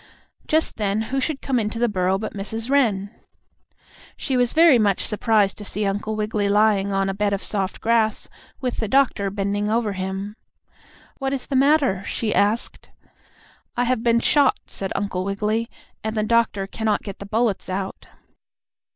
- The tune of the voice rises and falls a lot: No, average, 3.0 semitones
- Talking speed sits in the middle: Yes, average, 170 wpm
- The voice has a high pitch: Yes, high, 215 Hz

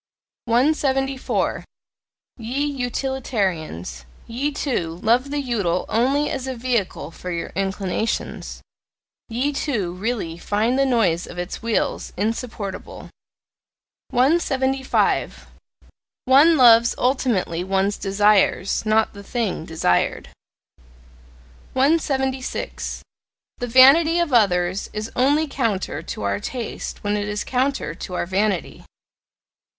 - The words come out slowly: Yes, slow, 105 wpm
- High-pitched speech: Yes, high, 230 Hz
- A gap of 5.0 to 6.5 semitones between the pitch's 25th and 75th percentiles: Yes, wide, 5.5 semitones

